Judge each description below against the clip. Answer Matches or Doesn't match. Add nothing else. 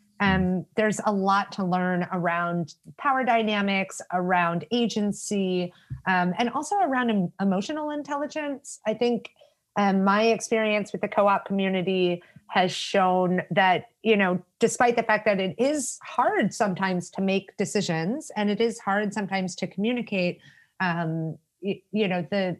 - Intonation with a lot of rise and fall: Doesn't match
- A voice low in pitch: Doesn't match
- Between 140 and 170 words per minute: Matches